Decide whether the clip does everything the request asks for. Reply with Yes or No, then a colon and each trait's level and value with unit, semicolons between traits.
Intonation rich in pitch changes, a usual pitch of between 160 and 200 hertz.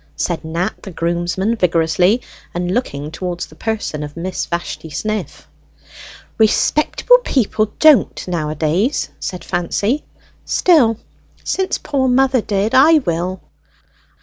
Yes: wide, 6.3 semitones; high, 190 Hz